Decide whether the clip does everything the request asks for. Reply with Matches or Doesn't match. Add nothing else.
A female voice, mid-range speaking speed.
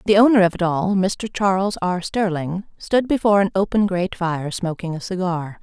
Matches